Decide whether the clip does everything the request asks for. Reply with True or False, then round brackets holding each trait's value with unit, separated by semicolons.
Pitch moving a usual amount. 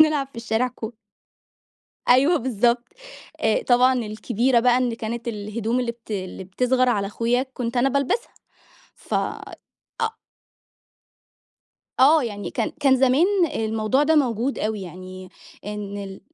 True (3.4 semitones)